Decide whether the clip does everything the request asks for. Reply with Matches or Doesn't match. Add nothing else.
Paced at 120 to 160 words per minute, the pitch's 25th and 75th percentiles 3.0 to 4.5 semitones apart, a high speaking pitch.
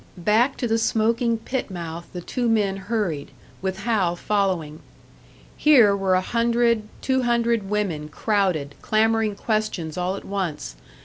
Matches